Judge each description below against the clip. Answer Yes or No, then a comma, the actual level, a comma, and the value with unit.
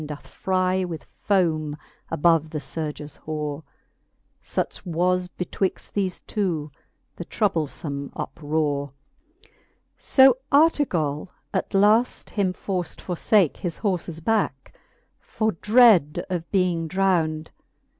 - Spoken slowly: Yes, slow, 105 wpm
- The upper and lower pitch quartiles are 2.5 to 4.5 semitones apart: Yes, average, 4.0 semitones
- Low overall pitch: No, medium, 175 Hz